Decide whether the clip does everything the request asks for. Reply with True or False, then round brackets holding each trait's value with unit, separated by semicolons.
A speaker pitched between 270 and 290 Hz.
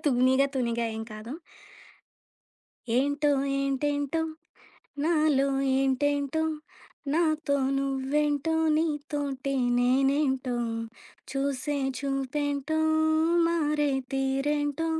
True (280 Hz)